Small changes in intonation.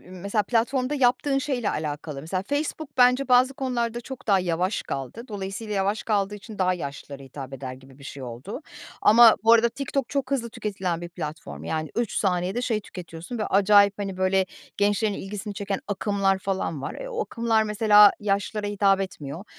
No: average, 4.4 semitones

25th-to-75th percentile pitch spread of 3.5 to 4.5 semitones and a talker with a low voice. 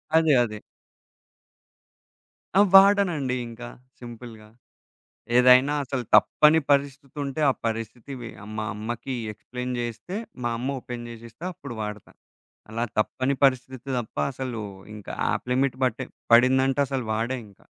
No: average, 2.8 semitones; low, 125 Hz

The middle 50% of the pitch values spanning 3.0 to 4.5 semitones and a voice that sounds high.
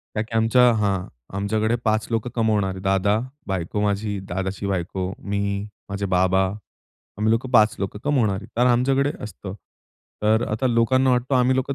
No: average, 3.4 semitones; low, 105 Hz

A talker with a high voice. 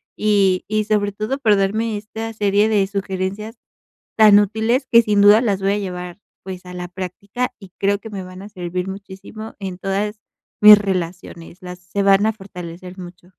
Yes: high, 200 Hz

